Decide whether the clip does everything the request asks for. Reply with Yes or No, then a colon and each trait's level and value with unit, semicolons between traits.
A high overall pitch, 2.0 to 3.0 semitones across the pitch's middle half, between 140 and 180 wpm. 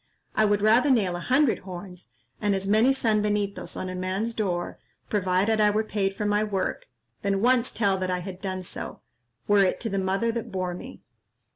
No: high, 205 Hz; average, 2.7 semitones; average, 195 wpm